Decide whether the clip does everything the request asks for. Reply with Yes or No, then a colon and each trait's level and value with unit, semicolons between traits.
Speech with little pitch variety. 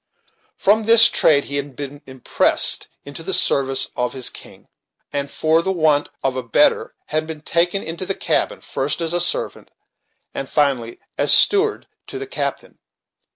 No: average, 4.2 semitones